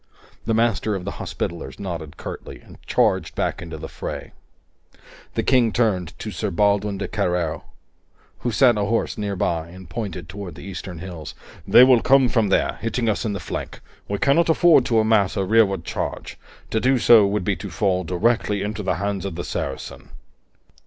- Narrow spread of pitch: No, average, 3.8 semitones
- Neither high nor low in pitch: No, low, 100 Hz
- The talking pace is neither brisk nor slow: Yes, average, 180 wpm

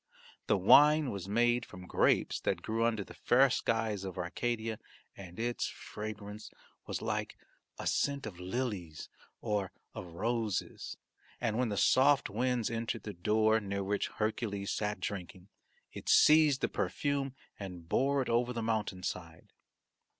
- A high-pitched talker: No, low, 110 Hz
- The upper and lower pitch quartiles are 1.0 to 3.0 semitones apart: No, average, 3.5 semitones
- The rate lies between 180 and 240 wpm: No, average, 150 wpm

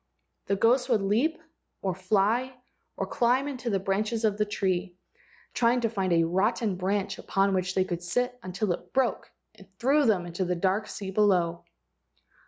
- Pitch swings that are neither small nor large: Yes, average, 4.0 semitones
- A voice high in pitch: Yes, high, 200 Hz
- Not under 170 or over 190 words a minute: Yes, average, 175 wpm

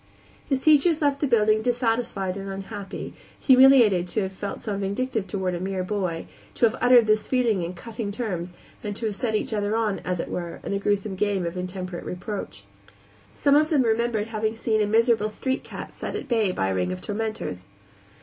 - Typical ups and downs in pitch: Yes, average, 3.7 semitones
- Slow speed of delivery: No, average, 200 wpm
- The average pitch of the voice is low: No, high, 210 Hz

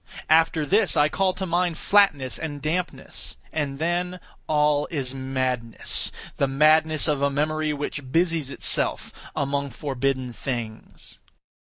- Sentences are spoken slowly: Yes, slow, 120 wpm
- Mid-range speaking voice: Yes, medium, 150 Hz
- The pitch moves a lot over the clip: No, average, 3.1 semitones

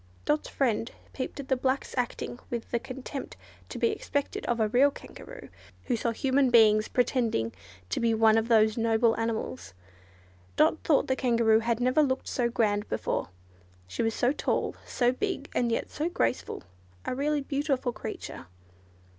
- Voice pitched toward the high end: Yes, high, 245 Hz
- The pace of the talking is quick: No, average, 165 wpm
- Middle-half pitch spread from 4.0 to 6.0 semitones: No, average, 3.3 semitones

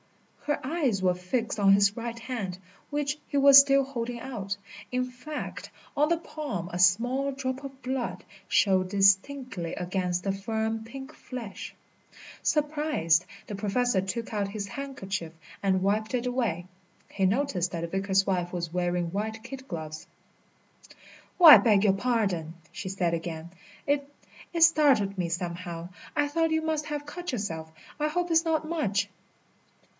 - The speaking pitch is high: Yes, high, 220 Hz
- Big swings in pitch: Yes, wide, 6.9 semitones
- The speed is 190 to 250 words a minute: No, average, 155 wpm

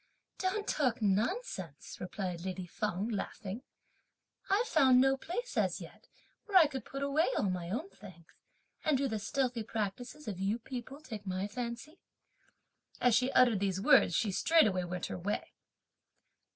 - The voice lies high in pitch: Yes, high, 230 Hz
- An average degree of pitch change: No, wide, 6.2 semitones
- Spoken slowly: No, average, 155 wpm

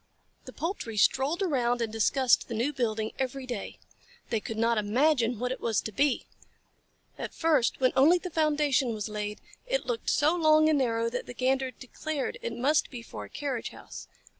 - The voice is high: Yes, very high, 255 Hz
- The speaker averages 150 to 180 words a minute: No, average, 190 wpm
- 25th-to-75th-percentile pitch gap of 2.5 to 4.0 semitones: No, average, 4.4 semitones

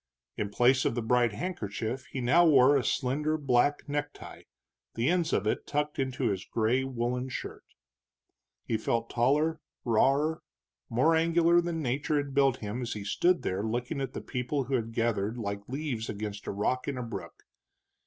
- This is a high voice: No, low, 125 Hz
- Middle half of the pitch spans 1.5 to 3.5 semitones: No, average, 4.3 semitones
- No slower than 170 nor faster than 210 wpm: Yes, average, 175 wpm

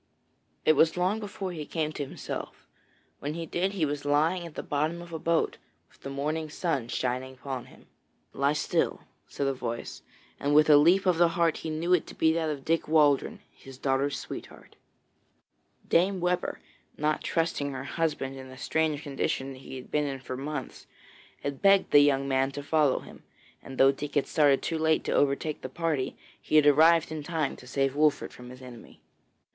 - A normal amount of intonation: Yes, average, 3.2 semitones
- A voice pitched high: No, medium, 150 Hz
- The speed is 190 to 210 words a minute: Yes, average, 195 wpm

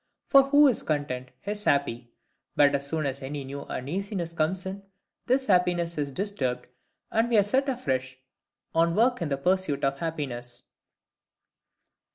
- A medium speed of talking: Yes, average, 155 wpm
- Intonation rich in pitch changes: Yes, wide, 6.4 semitones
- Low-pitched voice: No, medium, 165 Hz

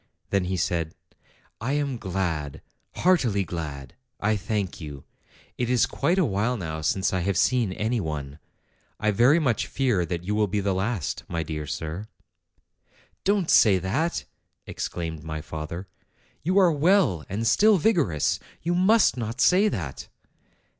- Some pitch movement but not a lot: No, wide, 7.9 semitones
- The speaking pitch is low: Yes, low, 100 Hz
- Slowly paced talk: No, average, 155 wpm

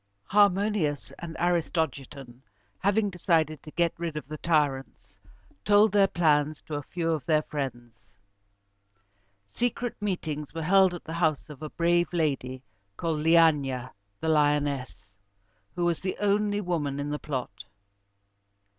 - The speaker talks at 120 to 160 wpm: Yes, average, 140 wpm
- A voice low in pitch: No, medium, 160 Hz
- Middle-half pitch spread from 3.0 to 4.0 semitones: Yes, average, 3.5 semitones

